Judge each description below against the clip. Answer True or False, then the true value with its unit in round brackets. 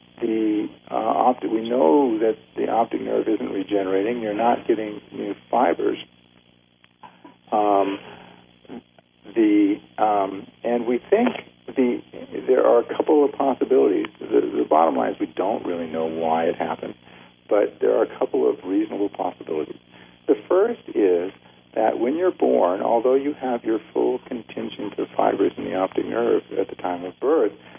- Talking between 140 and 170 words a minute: True (160 wpm)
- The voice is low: True (105 Hz)